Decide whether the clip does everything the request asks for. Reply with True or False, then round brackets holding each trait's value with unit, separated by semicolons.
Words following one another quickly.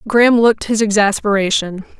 False (120 wpm)